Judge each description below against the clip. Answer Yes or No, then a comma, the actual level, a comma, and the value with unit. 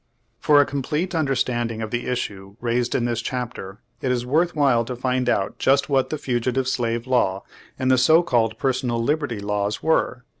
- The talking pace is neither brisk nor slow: Yes, average, 185 wpm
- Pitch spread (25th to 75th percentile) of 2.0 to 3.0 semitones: Yes, narrow, 2.6 semitones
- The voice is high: No, low, 125 Hz